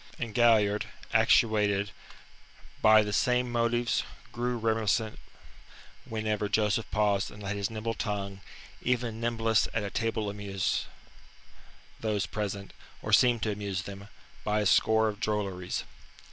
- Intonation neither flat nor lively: No, narrow, 2.0 semitones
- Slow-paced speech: Yes, slow, 130 wpm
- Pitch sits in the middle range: No, low, 105 Hz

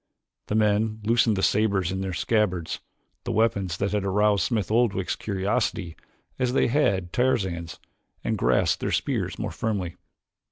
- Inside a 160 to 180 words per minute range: No, average, 150 wpm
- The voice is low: Yes, low, 100 Hz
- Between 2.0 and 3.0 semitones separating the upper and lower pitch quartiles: Yes, average, 2.7 semitones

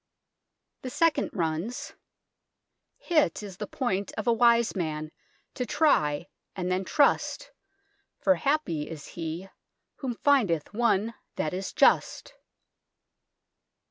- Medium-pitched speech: No, high, 205 Hz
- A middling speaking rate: No, slow, 115 wpm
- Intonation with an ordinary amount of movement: No, wide, 7.0 semitones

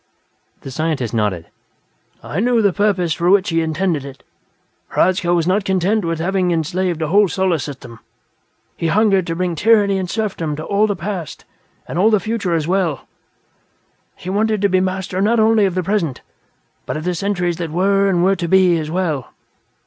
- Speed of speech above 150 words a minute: Yes, average, 185 wpm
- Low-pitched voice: No, medium, 180 Hz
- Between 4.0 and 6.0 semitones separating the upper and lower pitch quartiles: No, average, 3.3 semitones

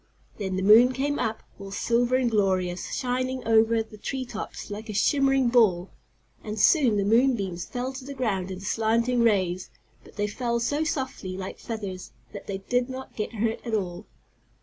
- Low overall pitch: No, high, 225 Hz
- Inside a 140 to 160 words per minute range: No, average, 185 wpm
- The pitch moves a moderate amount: Yes, average, 4.1 semitones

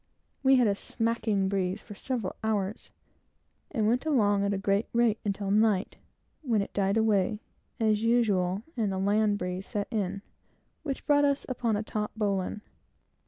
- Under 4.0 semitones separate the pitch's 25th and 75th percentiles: Yes, narrow, 2.4 semitones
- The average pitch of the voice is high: Yes, high, 210 Hz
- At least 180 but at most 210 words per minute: No, average, 165 wpm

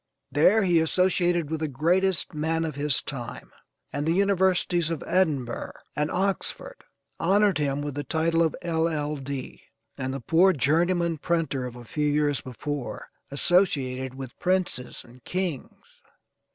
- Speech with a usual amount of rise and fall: Yes, average, 4.0 semitones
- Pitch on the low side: No, medium, 160 Hz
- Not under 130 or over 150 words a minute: Yes, average, 140 wpm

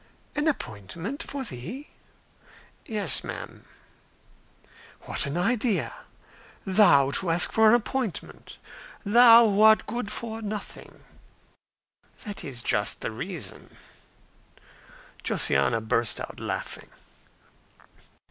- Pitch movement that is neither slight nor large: No, wide, 6.3 semitones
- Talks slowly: Yes, slow, 95 wpm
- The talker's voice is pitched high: Yes, high, 210 Hz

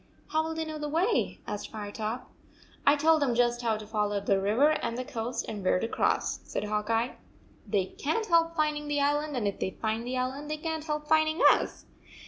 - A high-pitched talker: Yes, very high, 255 Hz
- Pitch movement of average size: No, wide, 5.9 semitones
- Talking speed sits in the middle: No, fast, 235 wpm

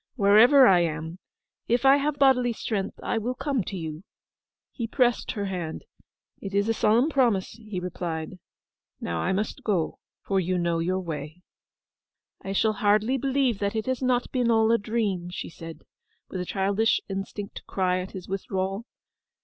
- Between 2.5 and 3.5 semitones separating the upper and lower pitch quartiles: No, average, 4.5 semitones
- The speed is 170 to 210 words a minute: Yes, average, 175 wpm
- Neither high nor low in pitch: No, high, 200 Hz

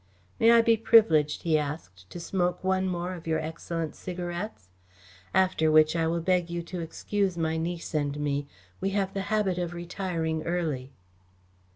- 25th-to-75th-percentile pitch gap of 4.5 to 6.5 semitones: No, average, 2.9 semitones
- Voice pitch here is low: No, medium, 170 Hz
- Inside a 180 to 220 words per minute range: No, average, 170 wpm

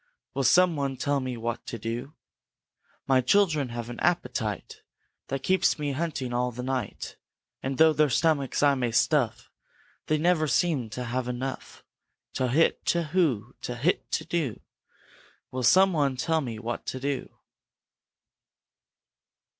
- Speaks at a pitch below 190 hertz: Yes, low, 135 Hz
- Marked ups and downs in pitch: No, average, 4.1 semitones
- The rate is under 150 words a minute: Yes, average, 140 wpm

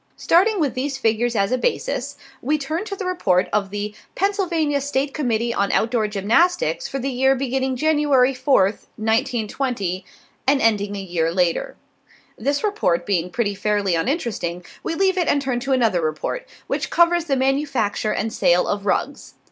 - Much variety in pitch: Yes, wide, 6.1 semitones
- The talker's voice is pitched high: Yes, very high, 255 Hz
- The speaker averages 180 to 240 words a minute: No, average, 165 wpm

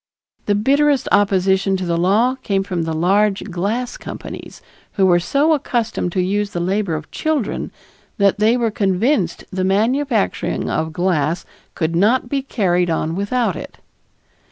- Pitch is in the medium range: No, high, 200 Hz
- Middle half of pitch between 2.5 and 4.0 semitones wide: No, average, 4.7 semitones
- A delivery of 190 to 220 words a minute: No, average, 155 wpm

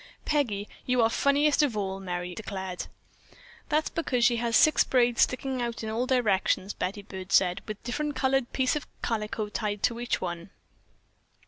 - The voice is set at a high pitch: Yes, high, 230 Hz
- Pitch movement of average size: Yes, average, 4.6 semitones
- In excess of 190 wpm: No, average, 175 wpm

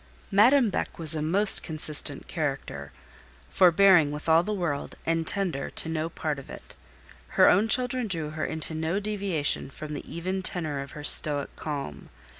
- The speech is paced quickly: No, average, 170 wpm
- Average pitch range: Yes, average, 4.3 semitones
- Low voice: No, medium, 160 Hz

